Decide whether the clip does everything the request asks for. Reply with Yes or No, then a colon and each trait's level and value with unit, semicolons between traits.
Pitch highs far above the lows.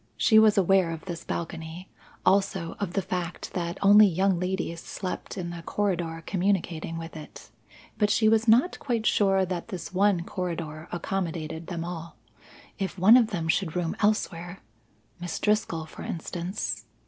No: average, 3.1 semitones